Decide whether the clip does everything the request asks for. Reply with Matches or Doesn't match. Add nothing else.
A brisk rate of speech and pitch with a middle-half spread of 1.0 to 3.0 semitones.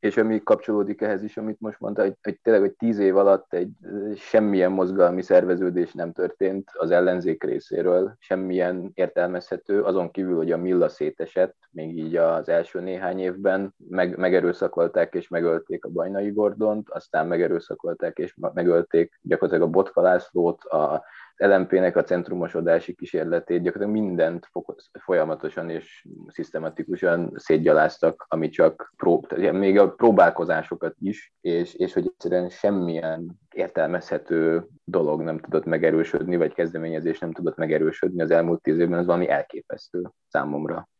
Doesn't match